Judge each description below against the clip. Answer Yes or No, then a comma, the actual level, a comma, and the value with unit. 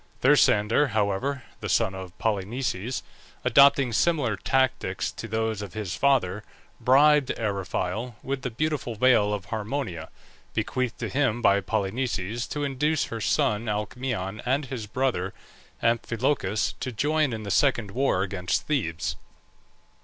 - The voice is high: No, low, 115 Hz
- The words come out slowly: Yes, slow, 130 wpm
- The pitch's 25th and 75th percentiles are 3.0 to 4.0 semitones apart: No, average, 4.8 semitones